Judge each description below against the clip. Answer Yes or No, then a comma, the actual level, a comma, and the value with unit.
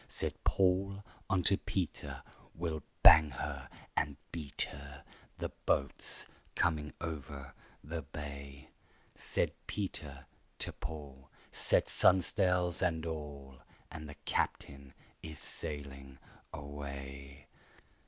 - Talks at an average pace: No, slow, 100 wpm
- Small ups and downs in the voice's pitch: No, average, 3.3 semitones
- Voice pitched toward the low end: Yes, very low, 75 Hz